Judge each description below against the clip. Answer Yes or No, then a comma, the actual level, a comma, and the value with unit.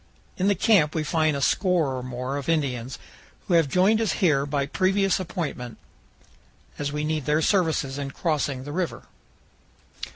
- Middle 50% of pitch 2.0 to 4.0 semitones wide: No, average, 4.6 semitones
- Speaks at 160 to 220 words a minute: Yes, average, 165 wpm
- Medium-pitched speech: Yes, medium, 150 Hz